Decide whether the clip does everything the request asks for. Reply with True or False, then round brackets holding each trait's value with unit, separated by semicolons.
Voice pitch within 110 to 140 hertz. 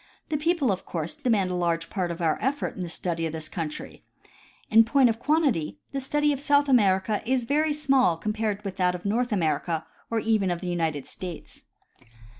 False (205 Hz)